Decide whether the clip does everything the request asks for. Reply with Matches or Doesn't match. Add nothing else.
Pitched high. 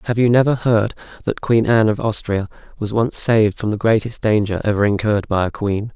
Doesn't match